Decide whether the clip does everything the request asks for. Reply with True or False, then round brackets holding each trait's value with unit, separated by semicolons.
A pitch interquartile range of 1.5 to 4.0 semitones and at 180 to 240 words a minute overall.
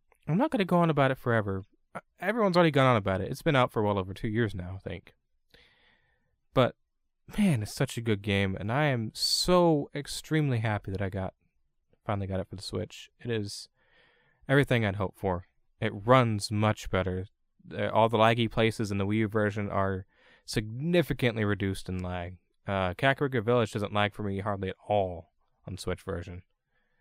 False (4.6 semitones; 190 wpm)